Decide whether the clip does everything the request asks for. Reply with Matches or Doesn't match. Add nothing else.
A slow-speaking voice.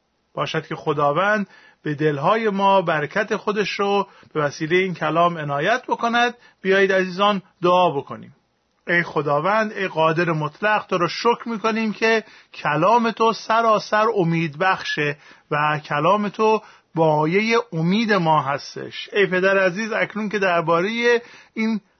Doesn't match